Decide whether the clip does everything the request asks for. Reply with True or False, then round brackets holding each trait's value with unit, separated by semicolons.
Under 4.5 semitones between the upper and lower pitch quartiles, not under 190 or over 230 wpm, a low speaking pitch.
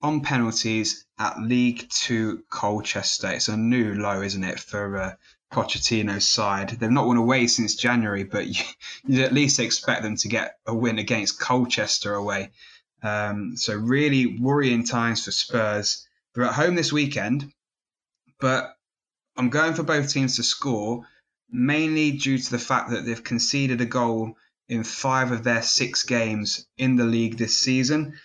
False (3.1 semitones; 165 wpm; 120 Hz)